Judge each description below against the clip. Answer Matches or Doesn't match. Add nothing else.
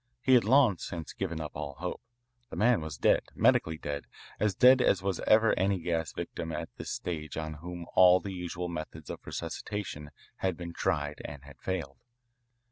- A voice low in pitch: Matches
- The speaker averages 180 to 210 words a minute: Matches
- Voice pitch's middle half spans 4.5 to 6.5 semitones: Doesn't match